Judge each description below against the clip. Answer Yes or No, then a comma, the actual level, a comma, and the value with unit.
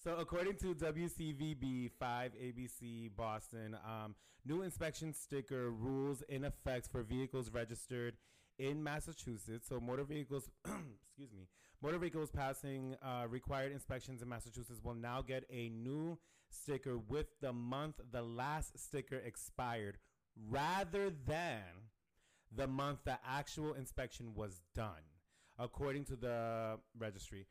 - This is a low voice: Yes, low, 130 Hz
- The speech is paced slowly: Yes, slow, 125 wpm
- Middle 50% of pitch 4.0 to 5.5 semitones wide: No, average, 3.5 semitones